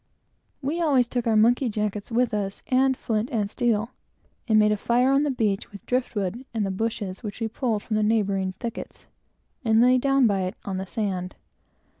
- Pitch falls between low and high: No, high, 220 Hz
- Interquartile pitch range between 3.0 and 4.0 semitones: Yes, average, 3.3 semitones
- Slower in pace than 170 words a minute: No, average, 195 wpm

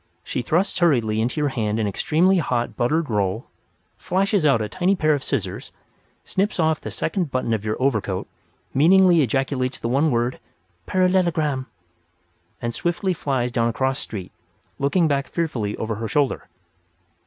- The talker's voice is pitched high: No, low, 135 Hz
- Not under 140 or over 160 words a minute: Yes, average, 155 wpm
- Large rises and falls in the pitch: Yes, wide, 6.2 semitones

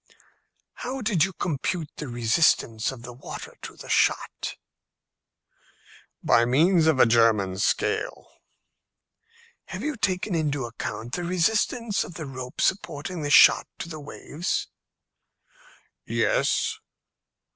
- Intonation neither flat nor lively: No, wide, 7.0 semitones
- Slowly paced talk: Yes, slow, 120 wpm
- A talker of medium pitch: Yes, medium, 155 Hz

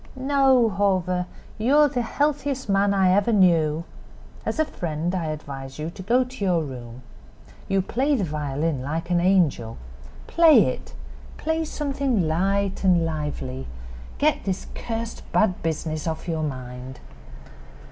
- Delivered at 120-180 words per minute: Yes, average, 145 wpm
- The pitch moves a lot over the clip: Yes, wide, 7.2 semitones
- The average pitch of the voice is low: No, medium, 185 Hz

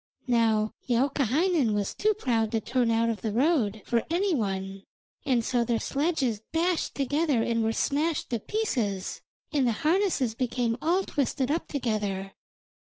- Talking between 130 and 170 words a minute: Yes, average, 155 wpm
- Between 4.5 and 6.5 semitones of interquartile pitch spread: Yes, wide, 5.4 semitones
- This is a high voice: Yes, high, 245 Hz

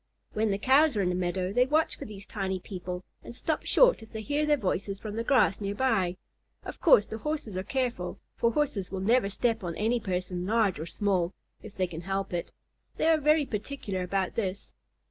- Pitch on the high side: Yes, high, 205 Hz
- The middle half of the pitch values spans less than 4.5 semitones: No, average, 5.0 semitones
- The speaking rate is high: Yes, fast, 215 wpm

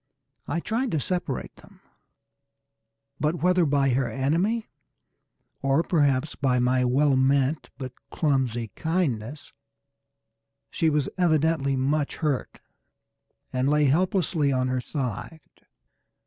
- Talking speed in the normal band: No, slow, 110 wpm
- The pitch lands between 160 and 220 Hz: No, medium, 140 Hz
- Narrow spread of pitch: No, average, 3.7 semitones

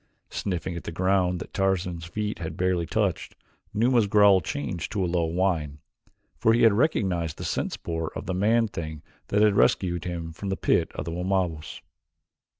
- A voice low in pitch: Yes, very low, 90 Hz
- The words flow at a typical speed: Yes, average, 180 wpm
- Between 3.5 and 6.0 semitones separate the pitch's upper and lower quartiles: No, average, 3.1 semitones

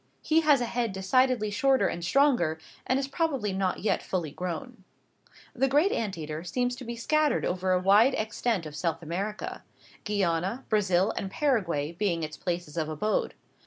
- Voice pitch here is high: Yes, high, 205 Hz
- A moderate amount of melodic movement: No, wide, 6.6 semitones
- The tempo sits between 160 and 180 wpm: Yes, average, 170 wpm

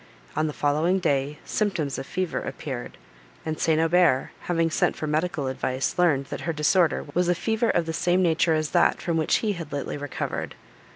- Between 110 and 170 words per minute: No, average, 190 wpm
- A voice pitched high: No, medium, 160 Hz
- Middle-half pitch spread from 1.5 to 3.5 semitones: Yes, average, 3.2 semitones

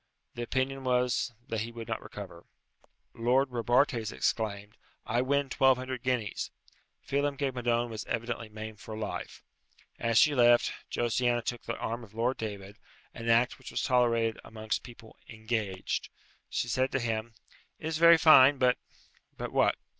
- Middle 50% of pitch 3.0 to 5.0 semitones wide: No, narrow, 2.5 semitones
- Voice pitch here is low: Yes, low, 120 Hz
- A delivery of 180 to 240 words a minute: No, average, 160 wpm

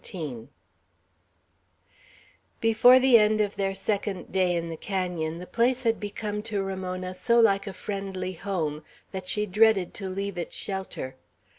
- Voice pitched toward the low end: No, high, 195 Hz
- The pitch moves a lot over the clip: No, narrow, 2.6 semitones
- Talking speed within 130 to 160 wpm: Yes, average, 150 wpm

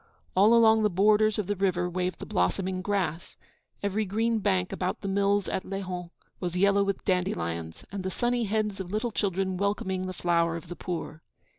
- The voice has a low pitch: No, high, 190 Hz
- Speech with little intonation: Yes, narrow, 2.3 semitones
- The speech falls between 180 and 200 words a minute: Yes, average, 185 wpm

